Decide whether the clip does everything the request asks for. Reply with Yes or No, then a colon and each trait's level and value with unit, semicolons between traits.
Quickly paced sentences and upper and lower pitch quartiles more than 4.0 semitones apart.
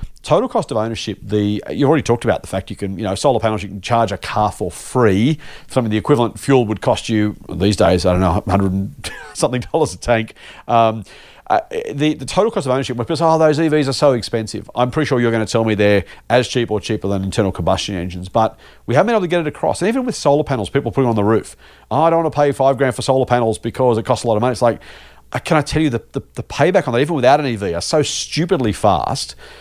Yes: fast, 270 wpm; average, 4.8 semitones